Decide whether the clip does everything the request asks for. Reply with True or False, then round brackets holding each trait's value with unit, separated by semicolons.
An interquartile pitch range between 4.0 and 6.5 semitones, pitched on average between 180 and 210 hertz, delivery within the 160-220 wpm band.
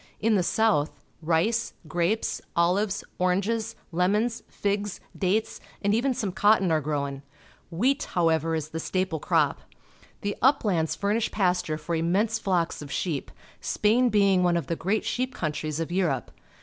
False (4.6 semitones; 185 Hz; 150 wpm)